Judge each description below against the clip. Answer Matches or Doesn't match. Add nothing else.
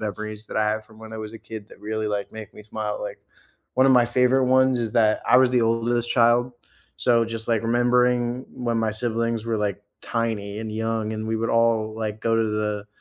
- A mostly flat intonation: Matches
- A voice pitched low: Matches